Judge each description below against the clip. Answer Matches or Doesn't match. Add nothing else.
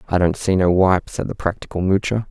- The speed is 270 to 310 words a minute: Doesn't match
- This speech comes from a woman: Doesn't match